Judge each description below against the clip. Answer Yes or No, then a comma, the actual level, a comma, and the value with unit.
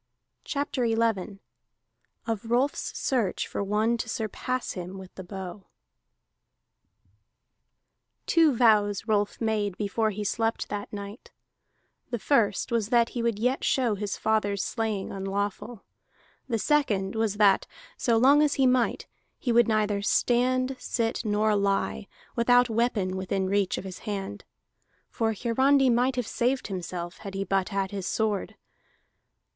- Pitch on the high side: Yes, high, 220 Hz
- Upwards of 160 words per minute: No, average, 140 wpm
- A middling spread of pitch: Yes, average, 3.2 semitones